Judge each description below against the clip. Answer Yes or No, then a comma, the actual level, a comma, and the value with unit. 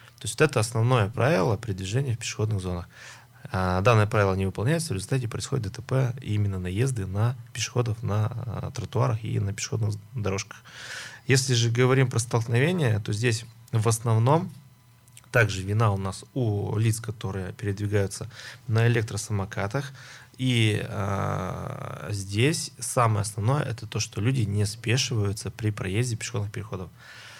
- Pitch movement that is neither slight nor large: Yes, average, 3.2 semitones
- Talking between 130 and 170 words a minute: Yes, average, 140 wpm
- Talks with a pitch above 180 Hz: No, low, 115 Hz